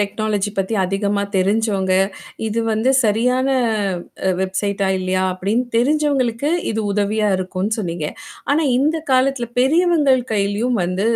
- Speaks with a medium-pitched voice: No, high, 215 Hz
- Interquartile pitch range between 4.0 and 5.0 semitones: Yes, average, 4.5 semitones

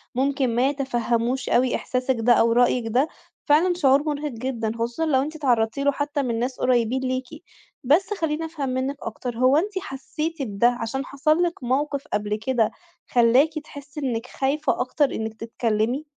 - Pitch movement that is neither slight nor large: Yes, average, 3.6 semitones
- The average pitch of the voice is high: Yes, very high, 260 Hz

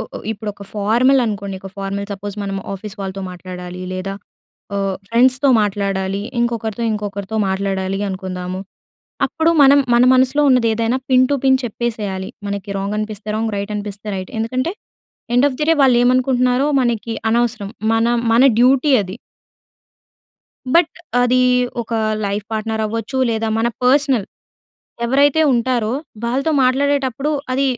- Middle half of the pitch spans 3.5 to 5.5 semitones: Yes, average, 4.2 semitones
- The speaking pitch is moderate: No, high, 225 Hz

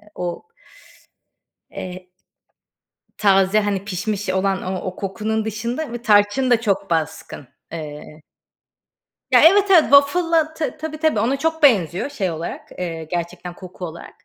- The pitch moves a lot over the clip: Yes, wide, 7.3 semitones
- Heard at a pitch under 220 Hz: Yes, high, 205 Hz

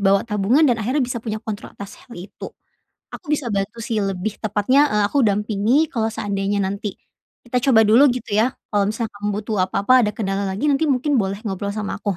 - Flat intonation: No, average, 3.6 semitones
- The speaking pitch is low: No, high, 215 Hz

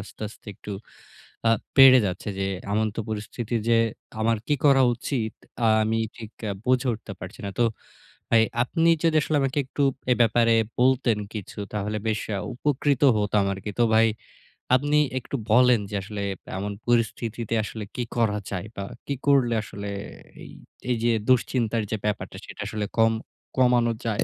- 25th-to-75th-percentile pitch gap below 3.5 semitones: Yes, average, 3.1 semitones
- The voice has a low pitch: Yes, low, 115 Hz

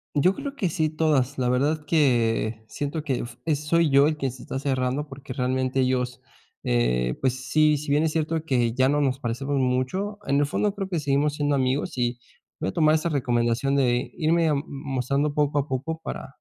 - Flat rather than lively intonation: No, average, 3.1 semitones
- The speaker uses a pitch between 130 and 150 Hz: Yes, medium, 140 Hz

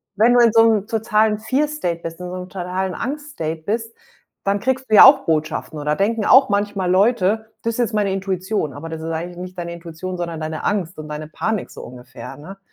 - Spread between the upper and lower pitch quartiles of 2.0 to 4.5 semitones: No, average, 5.0 semitones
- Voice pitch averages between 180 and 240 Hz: Yes, high, 190 Hz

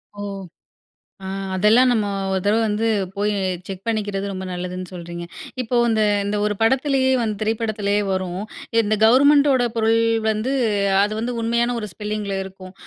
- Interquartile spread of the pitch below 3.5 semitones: Yes, average, 2.9 semitones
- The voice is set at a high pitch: Yes, high, 215 Hz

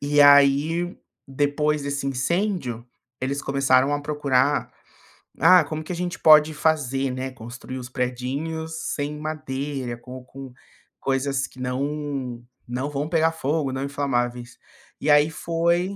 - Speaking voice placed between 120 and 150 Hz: Yes, medium, 140 Hz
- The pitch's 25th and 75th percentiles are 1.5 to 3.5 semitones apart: Yes, average, 2.8 semitones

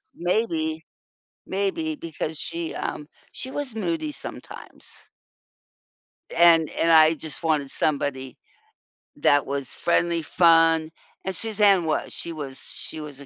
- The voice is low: No, medium, 165 Hz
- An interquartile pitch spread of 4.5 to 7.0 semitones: No, average, 3.6 semitones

